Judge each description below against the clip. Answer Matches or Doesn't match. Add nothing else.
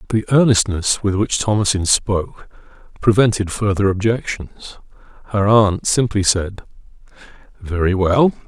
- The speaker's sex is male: Matches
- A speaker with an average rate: Doesn't match